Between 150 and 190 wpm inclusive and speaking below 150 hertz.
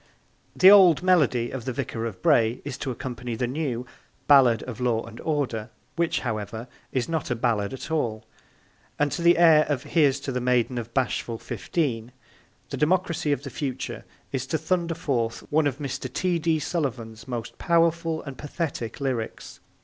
Yes: average, 175 wpm; low, 135 Hz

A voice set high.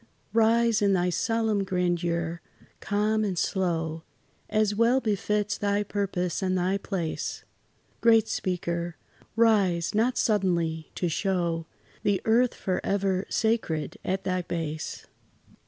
Yes: high, 195 Hz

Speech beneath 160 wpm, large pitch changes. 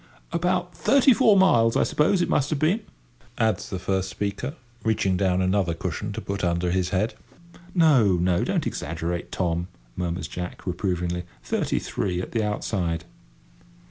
Yes: average, 150 wpm; wide, 6.6 semitones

